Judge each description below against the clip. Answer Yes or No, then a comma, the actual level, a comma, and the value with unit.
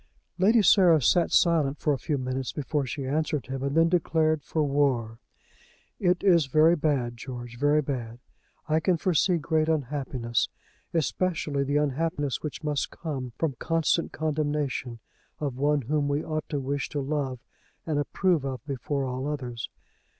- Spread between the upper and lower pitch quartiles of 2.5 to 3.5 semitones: Yes, average, 3.0 semitones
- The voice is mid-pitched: Yes, medium, 145 Hz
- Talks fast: No, average, 155 wpm